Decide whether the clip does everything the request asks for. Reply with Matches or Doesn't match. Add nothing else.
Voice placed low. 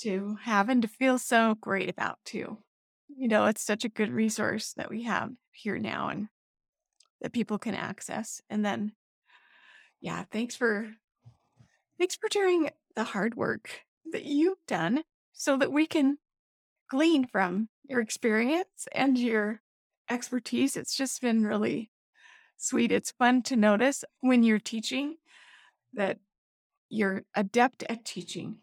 Doesn't match